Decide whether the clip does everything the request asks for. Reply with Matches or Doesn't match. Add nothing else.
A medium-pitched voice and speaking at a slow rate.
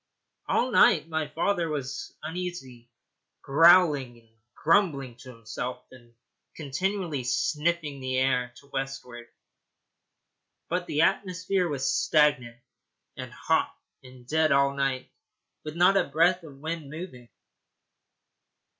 Matches